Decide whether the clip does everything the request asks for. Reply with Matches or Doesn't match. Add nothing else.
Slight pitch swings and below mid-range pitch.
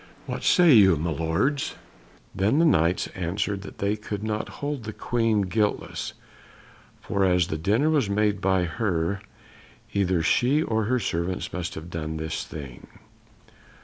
Doesn't match